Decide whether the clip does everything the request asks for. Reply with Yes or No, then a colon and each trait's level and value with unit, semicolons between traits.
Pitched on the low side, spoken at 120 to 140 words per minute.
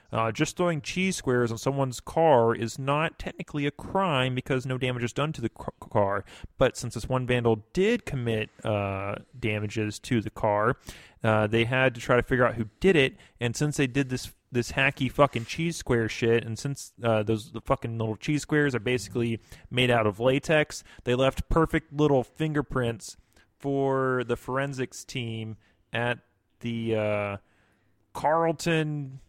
No: low, 125 Hz; average, 170 wpm